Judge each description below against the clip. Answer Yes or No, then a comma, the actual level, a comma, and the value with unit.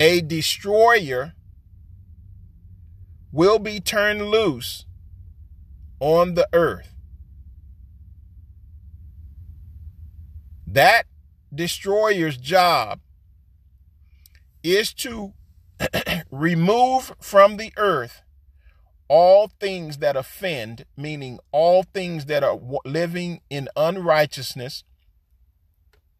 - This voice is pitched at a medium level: No, very low, 95 Hz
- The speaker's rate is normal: No, slow, 70 wpm